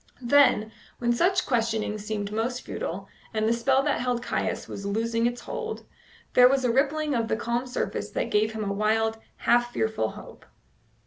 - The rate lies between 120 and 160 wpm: No, average, 180 wpm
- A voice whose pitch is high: Yes, high, 235 Hz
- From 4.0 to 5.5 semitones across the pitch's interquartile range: No, average, 2.7 semitones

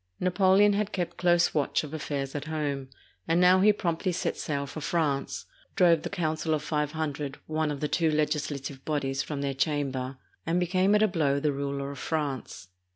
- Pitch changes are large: No, average, 3.5 semitones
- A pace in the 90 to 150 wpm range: No, average, 190 wpm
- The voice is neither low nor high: Yes, medium, 155 Hz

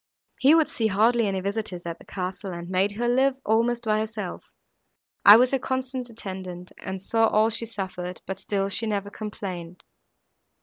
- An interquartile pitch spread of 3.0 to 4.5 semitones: Yes, average, 3.5 semitones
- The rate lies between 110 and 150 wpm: No, average, 175 wpm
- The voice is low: No, high, 210 Hz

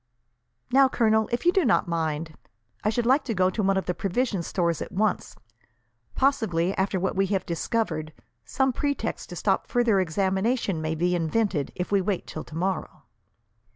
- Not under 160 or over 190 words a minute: Yes, average, 175 wpm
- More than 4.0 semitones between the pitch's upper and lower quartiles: Yes, average, 5.0 semitones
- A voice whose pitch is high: Yes, high, 195 Hz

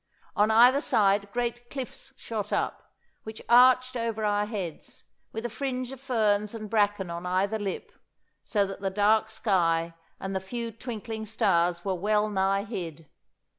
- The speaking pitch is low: No, high, 210 Hz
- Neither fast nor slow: Yes, average, 160 wpm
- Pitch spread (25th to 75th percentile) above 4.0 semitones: No, average, 3.2 semitones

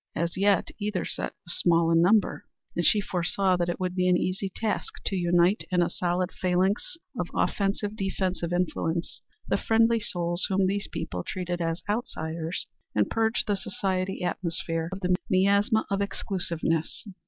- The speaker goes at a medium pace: Yes, average, 165 wpm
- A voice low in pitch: No, medium, 185 Hz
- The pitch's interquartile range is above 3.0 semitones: No, narrow, 2.4 semitones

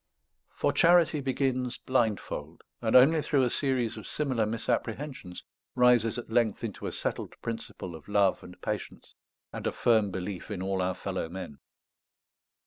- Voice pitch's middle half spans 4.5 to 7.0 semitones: Yes, average, 4.9 semitones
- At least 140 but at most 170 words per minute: Yes, average, 150 wpm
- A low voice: Yes, low, 115 Hz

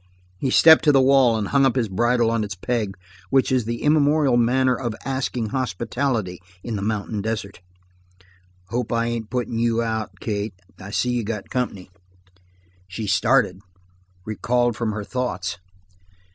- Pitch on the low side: Yes, low, 115 Hz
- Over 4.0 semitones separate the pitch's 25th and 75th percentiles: No, average, 3.3 semitones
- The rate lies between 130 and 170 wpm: Yes, average, 160 wpm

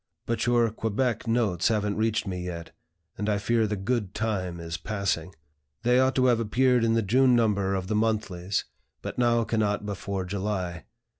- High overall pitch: No, low, 105 Hz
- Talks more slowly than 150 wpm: No, average, 175 wpm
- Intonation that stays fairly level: No, average, 3.2 semitones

